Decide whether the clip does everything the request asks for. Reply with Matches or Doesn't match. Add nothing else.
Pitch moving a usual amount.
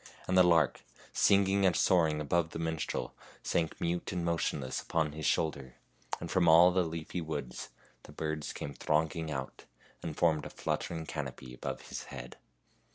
Doesn't match